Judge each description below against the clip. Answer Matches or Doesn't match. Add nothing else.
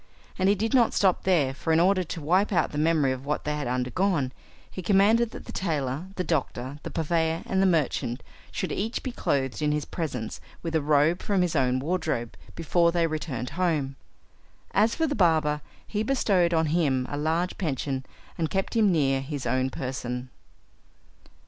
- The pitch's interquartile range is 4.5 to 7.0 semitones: Matches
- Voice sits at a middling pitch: Matches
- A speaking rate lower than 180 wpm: Doesn't match